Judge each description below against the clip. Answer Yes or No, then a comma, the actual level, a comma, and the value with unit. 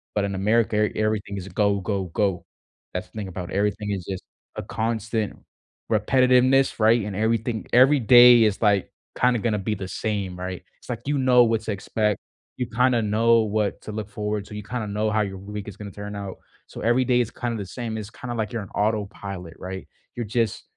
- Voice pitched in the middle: No, low, 105 Hz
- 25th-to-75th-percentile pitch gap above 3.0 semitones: No, narrow, 2.6 semitones